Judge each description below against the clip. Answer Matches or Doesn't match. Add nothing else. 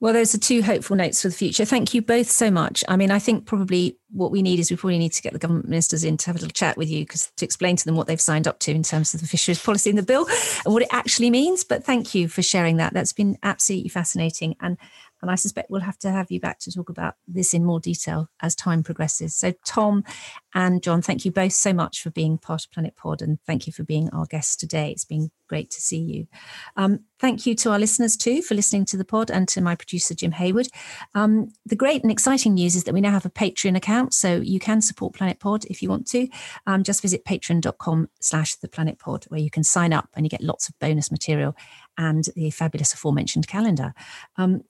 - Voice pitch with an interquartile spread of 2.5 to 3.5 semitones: Doesn't match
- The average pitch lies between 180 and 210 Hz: Matches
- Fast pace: Matches